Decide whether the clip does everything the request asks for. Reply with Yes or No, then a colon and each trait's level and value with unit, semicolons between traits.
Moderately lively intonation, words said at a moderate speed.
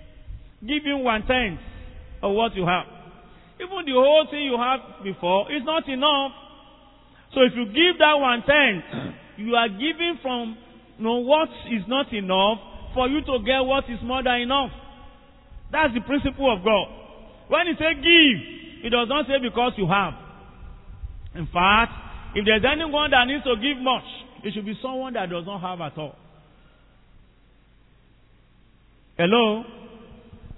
No: wide, 5.7 semitones; average, 160 wpm